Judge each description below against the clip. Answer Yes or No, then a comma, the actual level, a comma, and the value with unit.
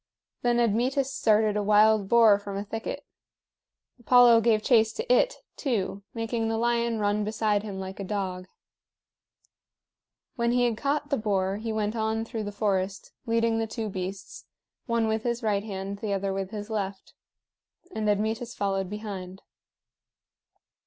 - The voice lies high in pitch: Yes, high, 215 Hz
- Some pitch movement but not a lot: No, narrow, 2.3 semitones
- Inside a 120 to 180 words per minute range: Yes, average, 155 wpm